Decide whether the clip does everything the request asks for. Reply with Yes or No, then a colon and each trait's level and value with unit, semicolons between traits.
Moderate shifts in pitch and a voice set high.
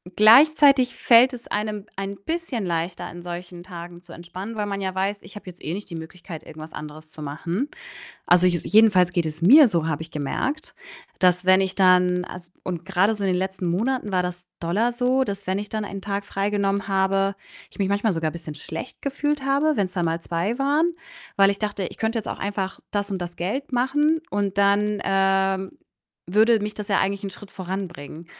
Yes: average, 3.2 semitones; high, 195 Hz